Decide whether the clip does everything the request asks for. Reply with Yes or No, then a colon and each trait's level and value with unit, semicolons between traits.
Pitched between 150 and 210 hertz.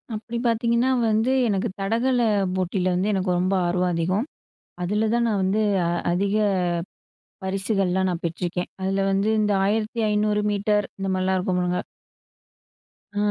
Yes: high, 195 Hz